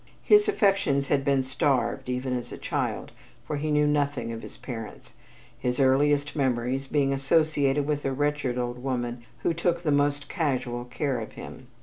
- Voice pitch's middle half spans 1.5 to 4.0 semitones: Yes, average, 2.8 semitones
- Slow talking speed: No, average, 175 wpm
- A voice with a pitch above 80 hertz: Yes, medium, 140 Hz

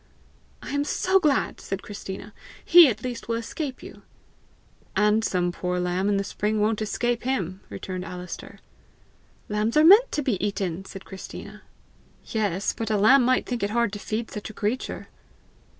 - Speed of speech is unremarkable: Yes, average, 170 wpm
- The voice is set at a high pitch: Yes, high, 215 Hz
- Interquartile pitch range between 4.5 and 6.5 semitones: No, average, 4.1 semitones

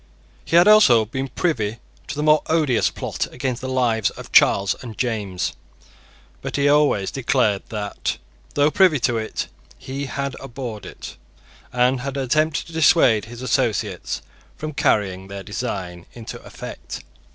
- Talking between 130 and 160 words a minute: Yes, average, 150 wpm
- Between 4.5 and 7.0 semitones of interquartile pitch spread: Yes, average, 4.8 semitones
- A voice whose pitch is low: Yes, low, 125 Hz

